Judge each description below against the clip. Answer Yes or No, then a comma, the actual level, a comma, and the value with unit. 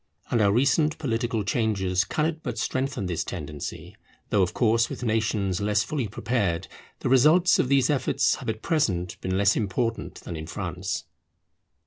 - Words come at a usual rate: Yes, average, 160 wpm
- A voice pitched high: No, low, 110 Hz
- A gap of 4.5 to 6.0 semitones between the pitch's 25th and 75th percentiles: Yes, average, 5.0 semitones